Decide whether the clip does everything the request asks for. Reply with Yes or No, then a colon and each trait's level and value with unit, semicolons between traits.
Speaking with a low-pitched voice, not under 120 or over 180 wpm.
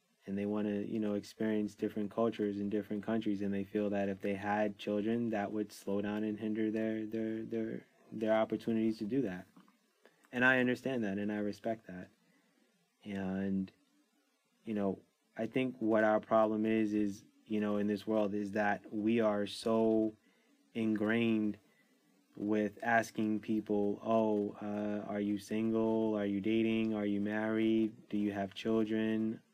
Yes: low, 105 Hz; average, 165 wpm